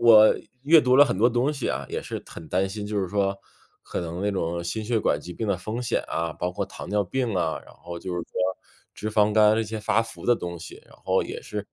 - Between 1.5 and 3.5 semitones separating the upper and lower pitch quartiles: No, average, 4.2 semitones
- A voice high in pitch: No, low, 105 Hz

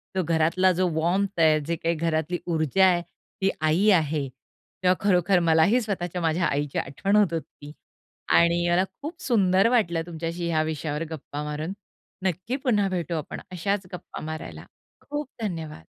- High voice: No, medium, 170 Hz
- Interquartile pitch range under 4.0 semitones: Yes, average, 3.2 semitones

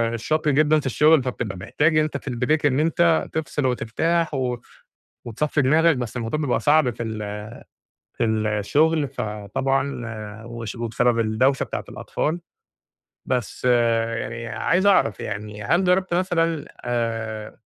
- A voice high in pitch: No, low, 130 Hz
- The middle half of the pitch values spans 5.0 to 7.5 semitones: Yes, average, 5.3 semitones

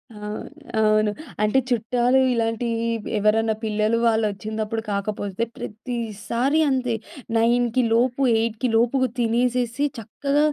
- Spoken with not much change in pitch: Yes, narrow, 2.2 semitones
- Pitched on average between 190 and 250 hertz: Yes, high, 230 Hz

